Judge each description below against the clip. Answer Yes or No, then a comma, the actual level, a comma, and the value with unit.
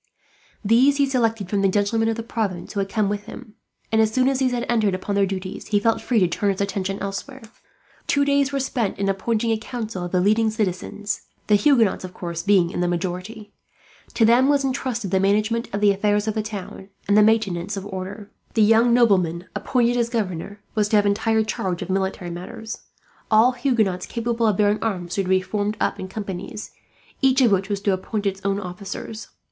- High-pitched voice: Yes, high, 210 Hz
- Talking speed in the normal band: No, fast, 215 wpm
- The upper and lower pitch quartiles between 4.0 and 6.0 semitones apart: No, average, 2.9 semitones